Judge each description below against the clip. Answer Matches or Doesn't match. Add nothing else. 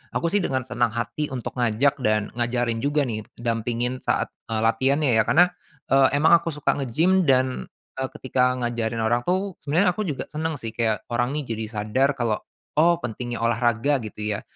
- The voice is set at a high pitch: Doesn't match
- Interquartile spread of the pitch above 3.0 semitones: Matches